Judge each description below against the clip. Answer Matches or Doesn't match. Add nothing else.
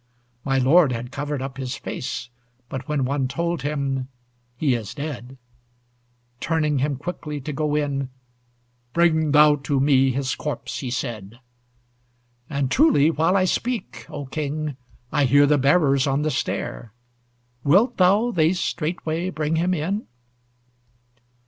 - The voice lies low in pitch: Doesn't match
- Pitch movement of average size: Matches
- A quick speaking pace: Doesn't match